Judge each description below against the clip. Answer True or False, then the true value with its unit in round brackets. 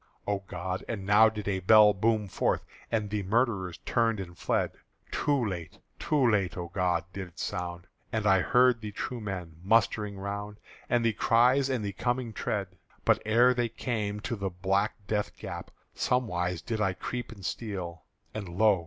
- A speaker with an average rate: True (180 wpm)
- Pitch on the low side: True (105 Hz)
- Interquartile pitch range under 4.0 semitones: True (3.4 semitones)